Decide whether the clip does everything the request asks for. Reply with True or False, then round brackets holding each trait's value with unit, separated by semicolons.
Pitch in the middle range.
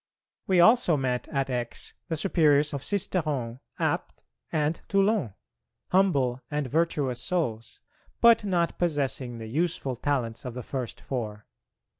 True (145 Hz)